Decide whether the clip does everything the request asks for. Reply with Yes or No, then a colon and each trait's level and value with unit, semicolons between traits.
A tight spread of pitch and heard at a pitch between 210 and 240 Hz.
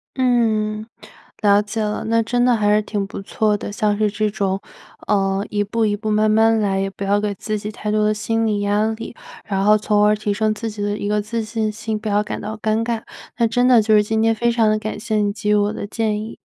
Yes: narrow, 1.2 semitones; high, 215 Hz